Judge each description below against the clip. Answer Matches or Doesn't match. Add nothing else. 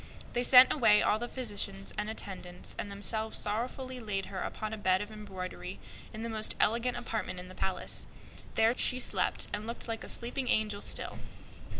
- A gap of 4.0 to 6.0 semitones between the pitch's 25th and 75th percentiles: Doesn't match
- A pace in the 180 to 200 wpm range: Doesn't match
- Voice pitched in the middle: Doesn't match